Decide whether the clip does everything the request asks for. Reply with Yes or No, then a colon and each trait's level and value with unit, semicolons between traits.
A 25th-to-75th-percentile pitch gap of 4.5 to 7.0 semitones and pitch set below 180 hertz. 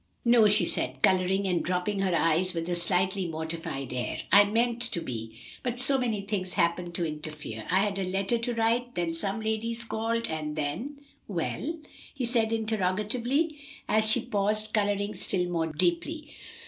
No: average, 5.1 semitones; high, 200 Hz